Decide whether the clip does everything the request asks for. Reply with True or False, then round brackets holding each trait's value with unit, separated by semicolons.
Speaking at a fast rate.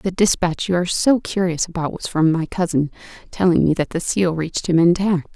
True (215 wpm)